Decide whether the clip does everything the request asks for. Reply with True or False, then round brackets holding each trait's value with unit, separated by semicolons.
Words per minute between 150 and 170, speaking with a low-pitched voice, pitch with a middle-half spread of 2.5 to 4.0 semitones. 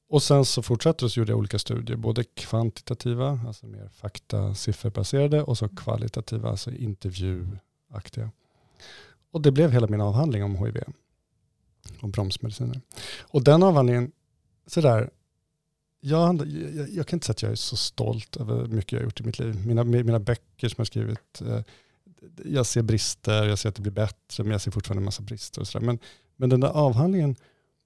False (180 wpm; 115 Hz; 3.4 semitones)